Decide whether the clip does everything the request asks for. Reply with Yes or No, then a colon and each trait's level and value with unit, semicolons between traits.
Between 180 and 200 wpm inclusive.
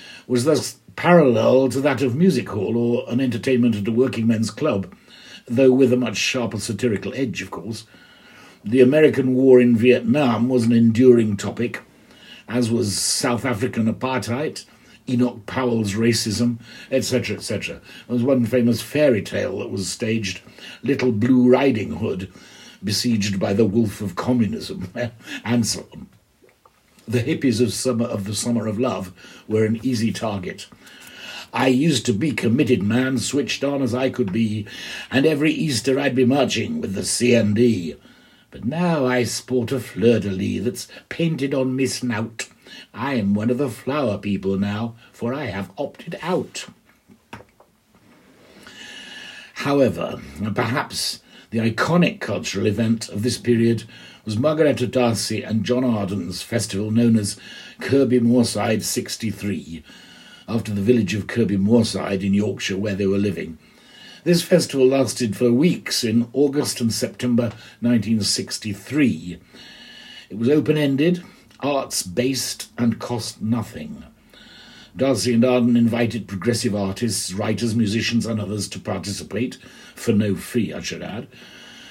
No: average, 140 wpm